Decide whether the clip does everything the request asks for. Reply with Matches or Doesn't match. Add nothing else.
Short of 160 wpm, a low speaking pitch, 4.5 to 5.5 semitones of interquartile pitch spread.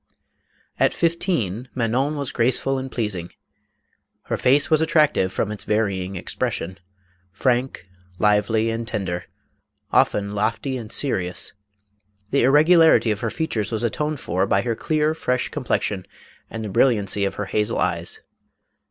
Matches